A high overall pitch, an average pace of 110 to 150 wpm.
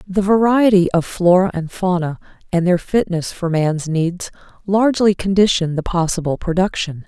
No: medium, 180 Hz; average, 145 wpm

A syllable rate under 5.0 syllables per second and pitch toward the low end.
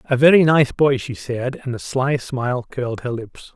Yes: 4.8 syllables/s; low, 130 Hz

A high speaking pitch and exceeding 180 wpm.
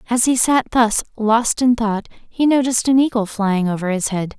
Yes: high, 230 Hz; fast, 205 wpm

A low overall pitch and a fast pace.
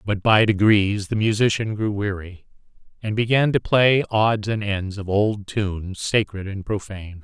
No: low, 105 Hz; average, 165 wpm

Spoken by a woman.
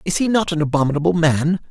No: male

